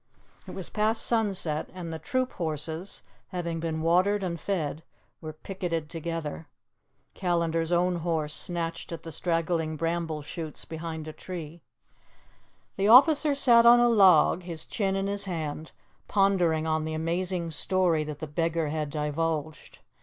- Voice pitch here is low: No, medium, 165 Hz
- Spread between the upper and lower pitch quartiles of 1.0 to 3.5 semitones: Yes, average, 2.9 semitones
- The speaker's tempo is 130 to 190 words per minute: Yes, average, 145 wpm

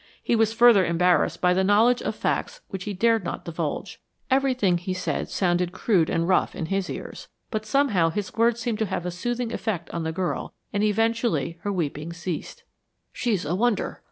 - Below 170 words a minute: No, average, 190 wpm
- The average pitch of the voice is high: Yes, high, 195 Hz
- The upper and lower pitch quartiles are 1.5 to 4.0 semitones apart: No, average, 4.6 semitones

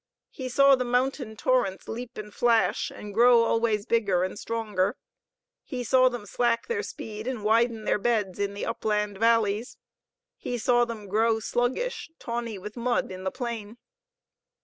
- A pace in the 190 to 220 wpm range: No, average, 160 wpm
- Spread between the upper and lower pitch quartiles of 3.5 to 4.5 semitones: No, average, 2.7 semitones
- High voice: Yes, high, 230 Hz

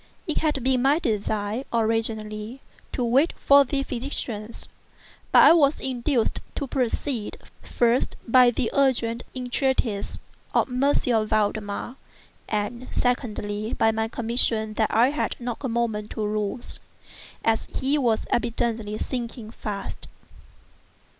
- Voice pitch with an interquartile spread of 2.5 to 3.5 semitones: Yes, average, 3.0 semitones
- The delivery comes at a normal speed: No, slow, 125 wpm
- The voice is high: Yes, high, 235 Hz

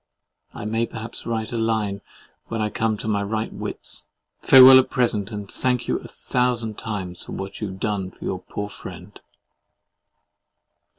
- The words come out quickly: No, average, 165 wpm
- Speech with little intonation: Yes, narrow, 2.3 semitones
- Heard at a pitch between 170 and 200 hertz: No, low, 110 Hz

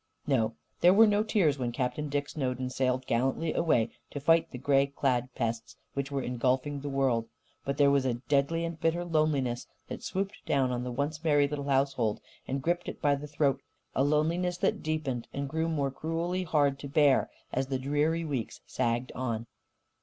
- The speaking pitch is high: No, medium, 140 Hz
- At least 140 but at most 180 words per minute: No, average, 190 wpm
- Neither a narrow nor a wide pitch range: Yes, average, 3.3 semitones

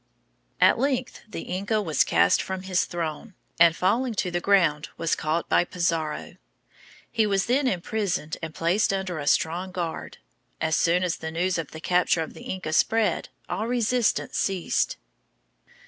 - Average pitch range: Yes, average, 3.9 semitones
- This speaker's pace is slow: No, average, 160 wpm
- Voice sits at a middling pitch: Yes, medium, 180 Hz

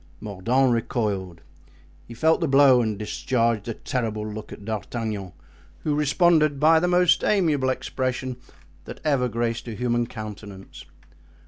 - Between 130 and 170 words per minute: Yes, slow, 135 wpm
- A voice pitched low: Yes, low, 120 Hz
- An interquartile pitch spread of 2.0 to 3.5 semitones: No, average, 4.6 semitones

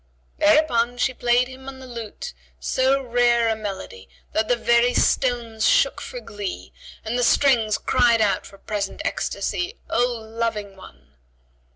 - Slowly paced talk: No, average, 150 wpm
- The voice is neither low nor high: No, high, 235 Hz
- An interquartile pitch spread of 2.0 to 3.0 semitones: Yes, narrow, 2.6 semitones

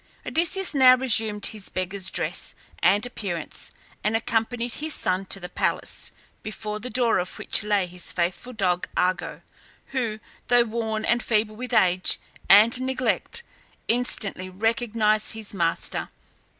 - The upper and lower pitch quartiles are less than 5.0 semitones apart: Yes, average, 4.0 semitones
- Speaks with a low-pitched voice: No, high, 215 Hz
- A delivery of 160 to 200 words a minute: No, slow, 135 wpm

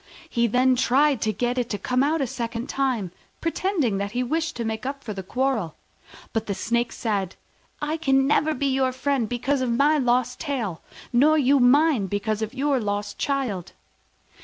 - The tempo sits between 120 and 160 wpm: No, average, 185 wpm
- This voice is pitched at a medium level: No, very high, 250 Hz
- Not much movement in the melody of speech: No, average, 4.0 semitones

